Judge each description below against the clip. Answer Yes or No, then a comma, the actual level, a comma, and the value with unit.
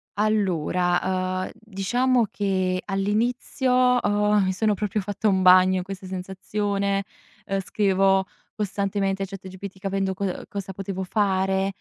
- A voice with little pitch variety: Yes, narrow, 1.6 semitones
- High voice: Yes, high, 195 Hz